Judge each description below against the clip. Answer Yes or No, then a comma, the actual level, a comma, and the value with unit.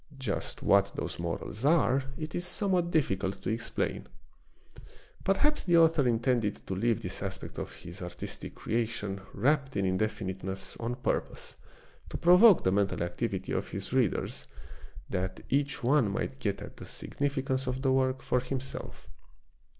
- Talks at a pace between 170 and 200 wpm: No, average, 150 wpm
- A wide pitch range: Yes, wide, 6.3 semitones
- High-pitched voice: No, low, 125 Hz